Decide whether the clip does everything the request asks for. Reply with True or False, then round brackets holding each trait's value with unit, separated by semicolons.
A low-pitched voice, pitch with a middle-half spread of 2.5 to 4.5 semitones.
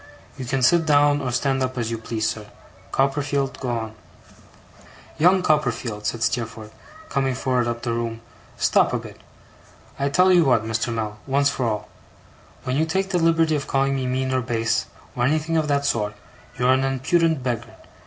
True (130 Hz; 3.7 semitones)